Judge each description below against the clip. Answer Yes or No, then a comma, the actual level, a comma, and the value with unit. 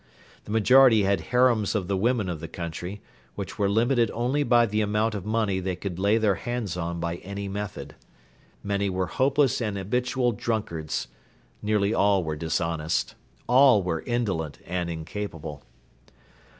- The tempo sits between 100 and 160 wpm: Yes, average, 155 wpm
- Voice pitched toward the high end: No, low, 100 Hz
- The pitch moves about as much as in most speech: Yes, average, 4.4 semitones